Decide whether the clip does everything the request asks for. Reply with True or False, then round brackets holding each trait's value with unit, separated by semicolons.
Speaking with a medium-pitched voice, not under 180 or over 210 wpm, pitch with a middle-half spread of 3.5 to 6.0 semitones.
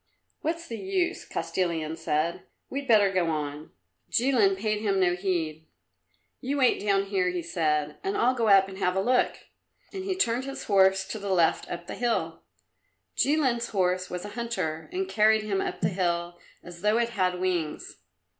False (195 Hz; 185 wpm; 5.1 semitones)